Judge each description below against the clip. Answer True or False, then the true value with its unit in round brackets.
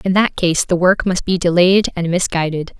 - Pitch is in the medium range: True (180 Hz)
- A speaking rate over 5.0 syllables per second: False (4.9 syllables/s)